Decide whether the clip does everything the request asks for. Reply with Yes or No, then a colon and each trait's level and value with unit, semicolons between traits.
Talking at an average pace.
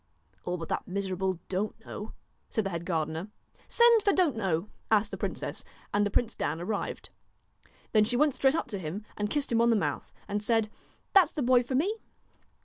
No: fast, 210 wpm